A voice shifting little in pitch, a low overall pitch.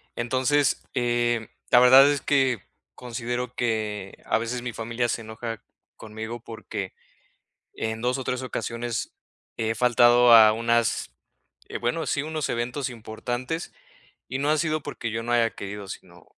Yes: narrow, 2.0 semitones; low, 120 Hz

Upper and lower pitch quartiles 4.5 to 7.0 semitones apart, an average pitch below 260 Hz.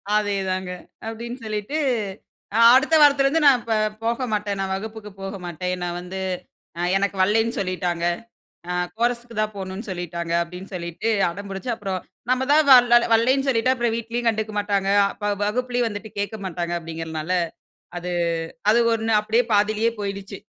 No: average, 3.7 semitones; high, 205 Hz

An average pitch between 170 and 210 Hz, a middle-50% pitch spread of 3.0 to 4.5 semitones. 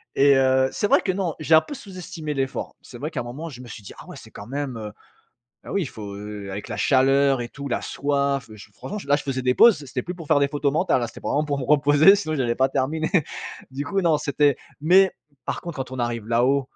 No: medium, 140 Hz; average, 3.6 semitones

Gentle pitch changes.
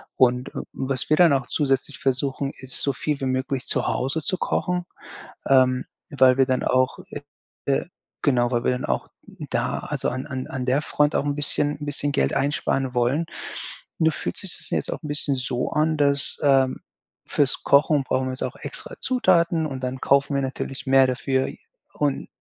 Yes: narrow, 2.2 semitones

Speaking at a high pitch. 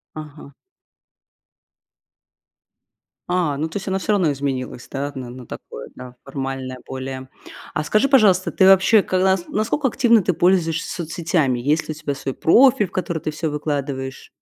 No: medium, 155 Hz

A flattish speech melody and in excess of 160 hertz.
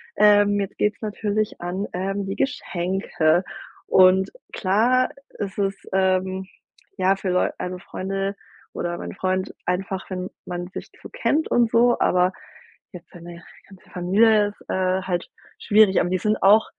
Yes: narrow, 2.0 semitones; high, 190 Hz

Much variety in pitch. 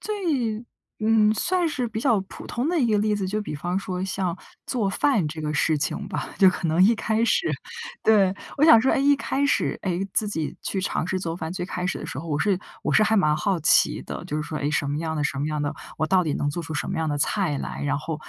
Yes: wide, 5.8 semitones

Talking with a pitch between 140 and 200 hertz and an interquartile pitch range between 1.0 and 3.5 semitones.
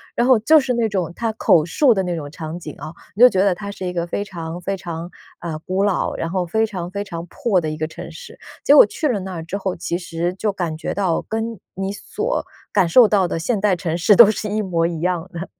No: medium, 185 Hz; average, 3.9 semitones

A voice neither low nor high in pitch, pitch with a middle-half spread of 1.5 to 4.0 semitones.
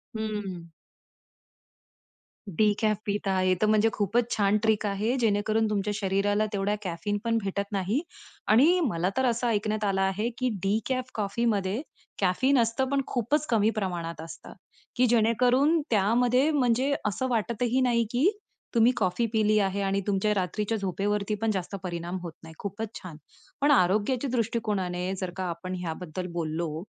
No: high, 210 Hz; average, 3.4 semitones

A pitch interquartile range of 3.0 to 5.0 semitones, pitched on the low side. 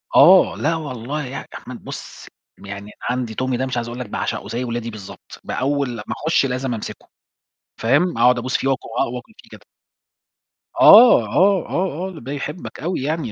Yes: average, 4.7 semitones; low, 130 Hz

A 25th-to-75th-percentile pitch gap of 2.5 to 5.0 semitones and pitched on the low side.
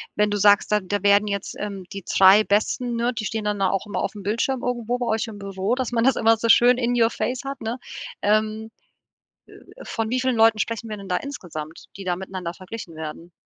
No: average, 2.9 semitones; high, 215 Hz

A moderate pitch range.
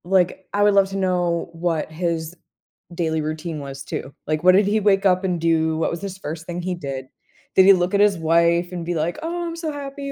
Yes: average, 3.2 semitones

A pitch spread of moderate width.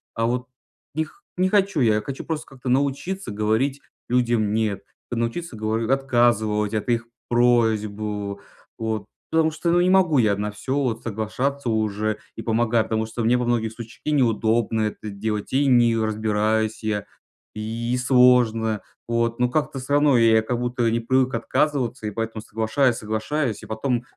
Yes: average, 3.0 semitones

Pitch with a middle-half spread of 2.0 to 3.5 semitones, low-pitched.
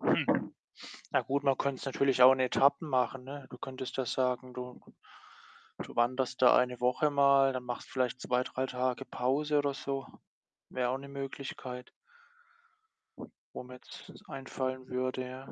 No: narrow, 1.4 semitones; low, 130 Hz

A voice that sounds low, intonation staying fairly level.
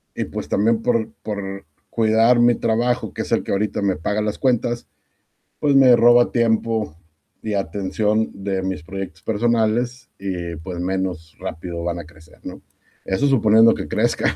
No: low, 105 Hz; average, 3.6 semitones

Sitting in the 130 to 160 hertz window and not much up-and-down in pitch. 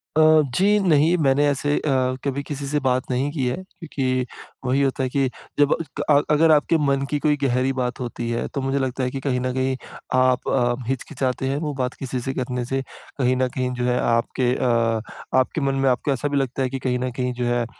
Yes: low, 135 Hz; narrow, 2.1 semitones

